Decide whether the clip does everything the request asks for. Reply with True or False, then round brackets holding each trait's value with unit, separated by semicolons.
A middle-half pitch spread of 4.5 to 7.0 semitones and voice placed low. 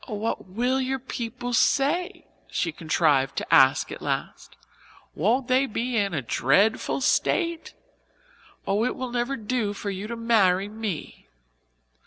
False (4.9 semitones; 225 Hz)